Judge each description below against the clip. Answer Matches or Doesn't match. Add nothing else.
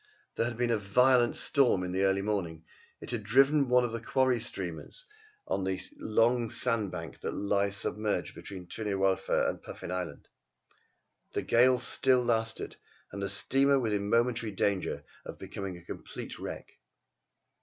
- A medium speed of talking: Matches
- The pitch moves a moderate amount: Matches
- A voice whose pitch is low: Matches